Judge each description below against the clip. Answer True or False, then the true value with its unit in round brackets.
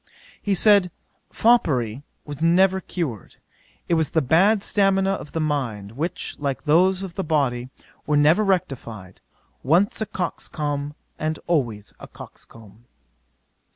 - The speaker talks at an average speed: False (130 wpm)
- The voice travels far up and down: True (6.2 semitones)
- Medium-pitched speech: True (155 Hz)